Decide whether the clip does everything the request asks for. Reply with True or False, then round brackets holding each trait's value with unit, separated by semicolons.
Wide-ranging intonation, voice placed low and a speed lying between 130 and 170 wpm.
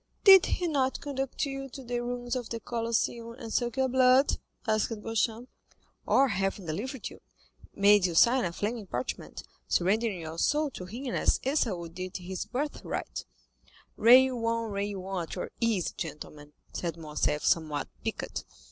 False (5.7 semitones; 230 Hz; 160 wpm)